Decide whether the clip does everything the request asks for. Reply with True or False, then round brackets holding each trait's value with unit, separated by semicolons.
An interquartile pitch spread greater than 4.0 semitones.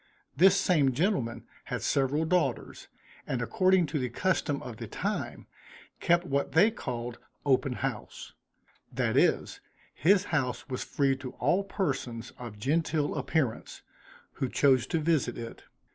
True (5.1 semitones)